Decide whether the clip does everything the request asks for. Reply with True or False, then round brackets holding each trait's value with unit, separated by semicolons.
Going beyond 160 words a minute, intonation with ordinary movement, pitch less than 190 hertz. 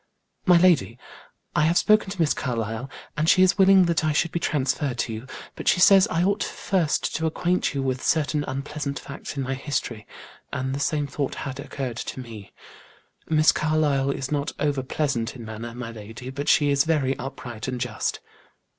True (190 wpm; 3.7 semitones; 140 Hz)